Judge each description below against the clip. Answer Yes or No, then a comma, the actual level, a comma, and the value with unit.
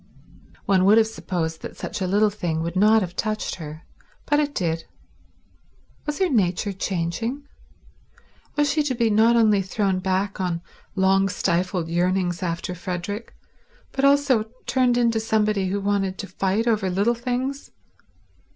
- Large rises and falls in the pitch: No, average, 4.0 semitones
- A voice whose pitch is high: Yes, high, 200 Hz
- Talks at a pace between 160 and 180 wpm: No, average, 150 wpm